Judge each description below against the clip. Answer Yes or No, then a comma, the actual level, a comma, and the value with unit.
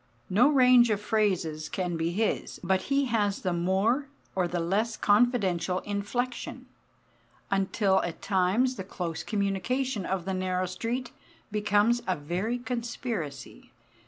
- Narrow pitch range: No, average, 4.5 semitones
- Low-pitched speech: No, high, 200 Hz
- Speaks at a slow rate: Yes, slow, 130 wpm